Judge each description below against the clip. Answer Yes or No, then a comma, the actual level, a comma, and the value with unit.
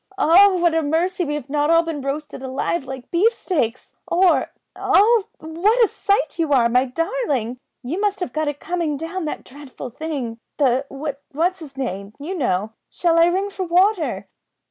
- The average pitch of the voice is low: No, very high, 315 Hz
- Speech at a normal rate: Yes, average, 175 wpm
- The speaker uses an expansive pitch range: No, average, 4.9 semitones